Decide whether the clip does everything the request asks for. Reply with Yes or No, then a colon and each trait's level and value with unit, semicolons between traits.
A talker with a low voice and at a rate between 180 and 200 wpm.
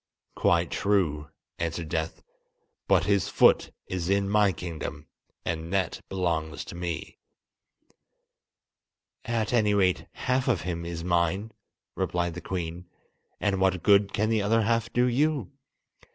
No: very low, 95 Hz; slow, 135 wpm